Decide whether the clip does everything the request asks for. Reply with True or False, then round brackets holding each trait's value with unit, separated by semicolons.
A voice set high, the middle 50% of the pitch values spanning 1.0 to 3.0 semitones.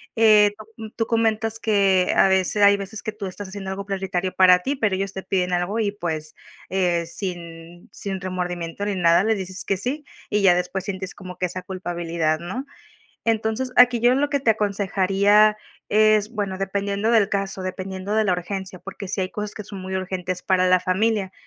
True (195 Hz; 2.5 semitones)